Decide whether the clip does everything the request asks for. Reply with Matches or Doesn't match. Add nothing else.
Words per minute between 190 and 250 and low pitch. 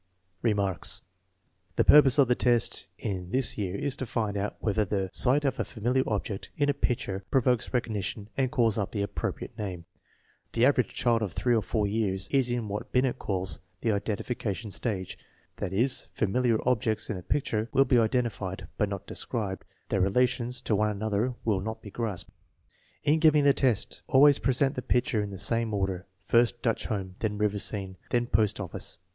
Matches